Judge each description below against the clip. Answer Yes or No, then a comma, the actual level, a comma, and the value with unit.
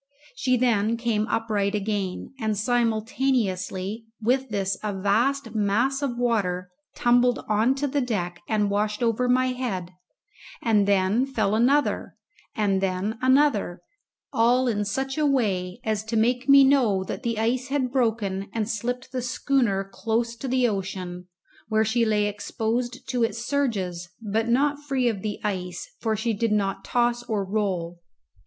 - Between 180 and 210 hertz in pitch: No, high, 225 Hz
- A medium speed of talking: Yes, average, 155 wpm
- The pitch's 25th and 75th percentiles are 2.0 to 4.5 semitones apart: Yes, average, 3.7 semitones